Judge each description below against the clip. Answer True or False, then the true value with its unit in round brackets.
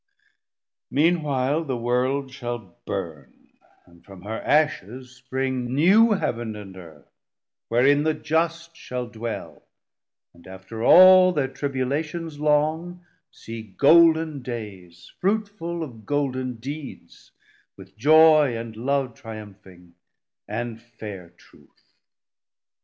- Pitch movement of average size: False (5.9 semitones)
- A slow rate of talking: True (110 wpm)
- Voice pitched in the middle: False (130 Hz)